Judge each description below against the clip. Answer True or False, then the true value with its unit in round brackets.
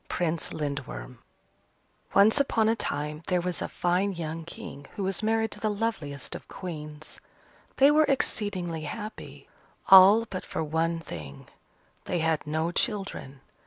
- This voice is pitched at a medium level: True (175 Hz)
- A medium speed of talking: True (145 wpm)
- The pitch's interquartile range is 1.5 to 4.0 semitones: False (5.5 semitones)